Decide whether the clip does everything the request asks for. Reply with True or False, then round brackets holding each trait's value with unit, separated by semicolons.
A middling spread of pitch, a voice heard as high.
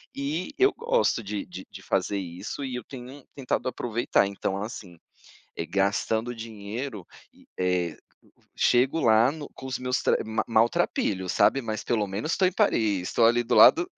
False (4.8 semitones; 115 Hz)